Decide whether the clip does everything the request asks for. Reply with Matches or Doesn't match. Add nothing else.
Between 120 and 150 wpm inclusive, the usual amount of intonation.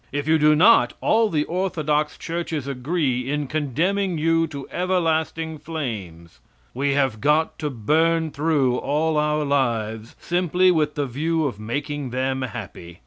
Matches